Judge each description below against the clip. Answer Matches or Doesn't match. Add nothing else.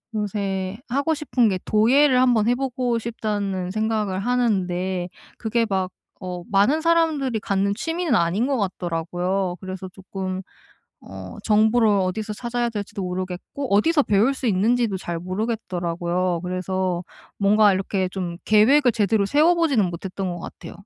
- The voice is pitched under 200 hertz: Doesn't match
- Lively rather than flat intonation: Doesn't match